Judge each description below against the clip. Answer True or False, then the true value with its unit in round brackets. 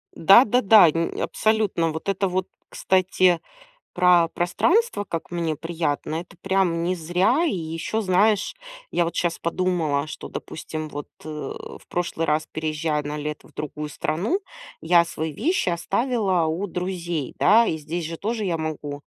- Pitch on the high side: False (170 Hz)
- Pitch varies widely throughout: False (3.3 semitones)